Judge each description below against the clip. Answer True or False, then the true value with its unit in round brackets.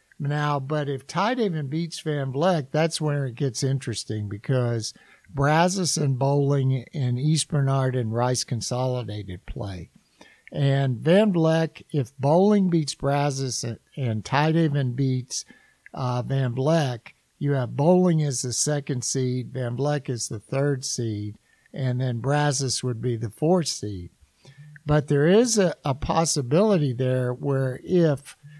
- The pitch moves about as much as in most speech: True (3.4 semitones)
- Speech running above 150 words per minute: False (145 wpm)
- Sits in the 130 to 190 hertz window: True (140 Hz)